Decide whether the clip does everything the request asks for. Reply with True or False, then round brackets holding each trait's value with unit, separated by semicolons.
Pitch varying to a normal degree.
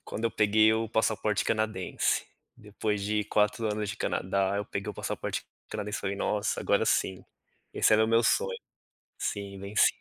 False (1.5 semitones)